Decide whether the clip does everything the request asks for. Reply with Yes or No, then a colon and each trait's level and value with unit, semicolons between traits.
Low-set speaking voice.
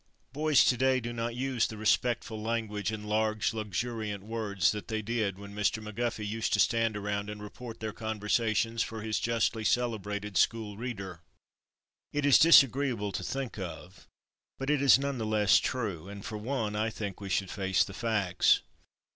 Yes: low, 110 Hz